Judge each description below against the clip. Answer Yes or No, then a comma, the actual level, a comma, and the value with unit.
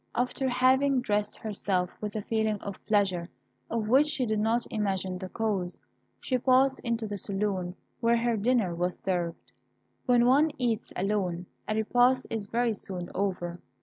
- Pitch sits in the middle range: No, high, 215 Hz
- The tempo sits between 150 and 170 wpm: Yes, average, 160 wpm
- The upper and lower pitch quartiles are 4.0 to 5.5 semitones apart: Yes, average, 4.3 semitones